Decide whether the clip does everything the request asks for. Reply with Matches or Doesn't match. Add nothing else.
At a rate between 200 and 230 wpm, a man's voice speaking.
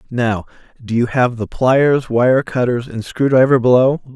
Doesn't match